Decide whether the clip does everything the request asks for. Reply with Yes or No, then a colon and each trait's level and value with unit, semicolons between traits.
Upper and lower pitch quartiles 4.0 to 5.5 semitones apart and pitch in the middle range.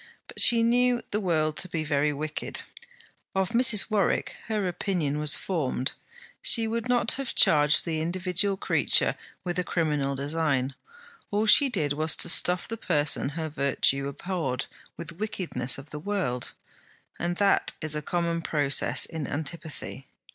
Yes: average, 5.0 semitones; medium, 165 Hz